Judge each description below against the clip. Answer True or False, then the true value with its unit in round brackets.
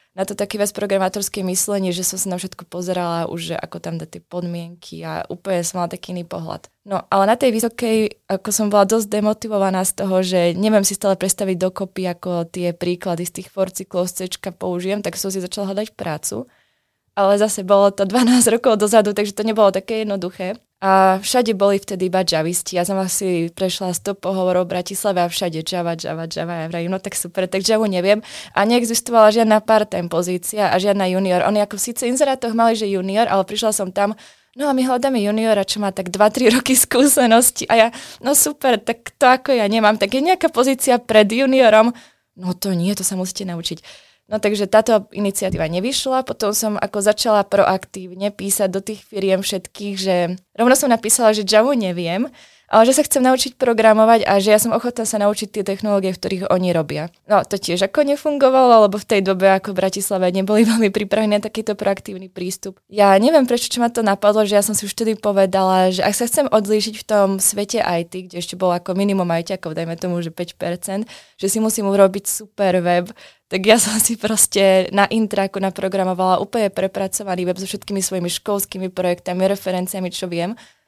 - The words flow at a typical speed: False (195 wpm)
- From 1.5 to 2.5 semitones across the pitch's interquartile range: False (2.9 semitones)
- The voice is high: True (200 Hz)